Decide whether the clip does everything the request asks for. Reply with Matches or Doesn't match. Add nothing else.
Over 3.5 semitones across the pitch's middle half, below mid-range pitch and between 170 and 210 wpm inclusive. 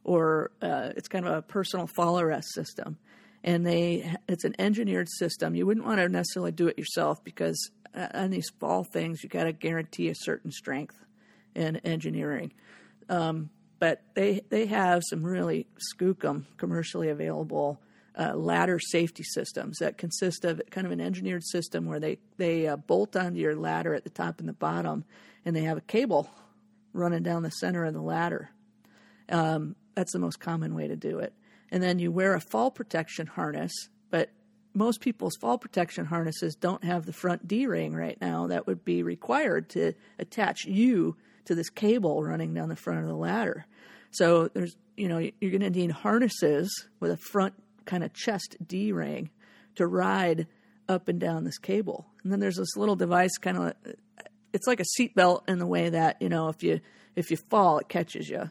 Doesn't match